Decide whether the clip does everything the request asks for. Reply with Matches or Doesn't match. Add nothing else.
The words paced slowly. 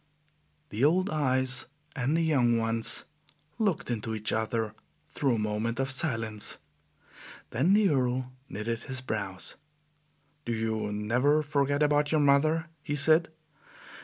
Matches